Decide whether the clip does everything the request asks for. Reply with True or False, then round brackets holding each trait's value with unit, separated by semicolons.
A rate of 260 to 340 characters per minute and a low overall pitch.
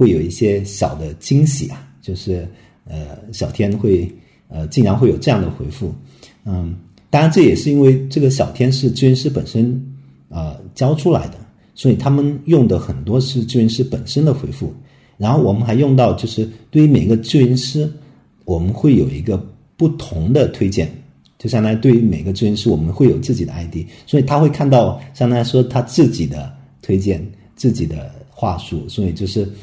True (275 characters per minute; 115 Hz)